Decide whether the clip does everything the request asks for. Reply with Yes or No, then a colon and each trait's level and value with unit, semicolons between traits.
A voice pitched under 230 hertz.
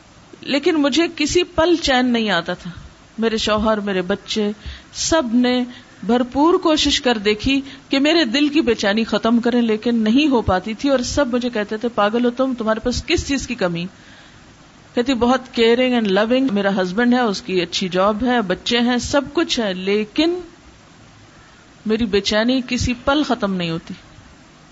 No: high, 240 Hz